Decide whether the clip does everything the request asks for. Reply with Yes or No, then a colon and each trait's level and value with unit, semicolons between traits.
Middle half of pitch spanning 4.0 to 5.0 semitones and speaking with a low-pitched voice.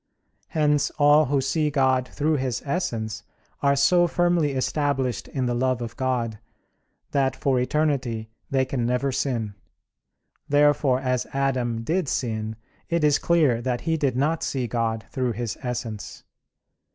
No: average, 3.2 semitones; low, 130 Hz